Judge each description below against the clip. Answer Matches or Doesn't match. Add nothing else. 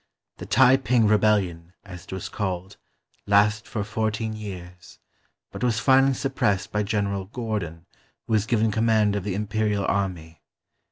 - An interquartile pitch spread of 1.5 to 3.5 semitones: Matches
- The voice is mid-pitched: Doesn't match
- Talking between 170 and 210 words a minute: Doesn't match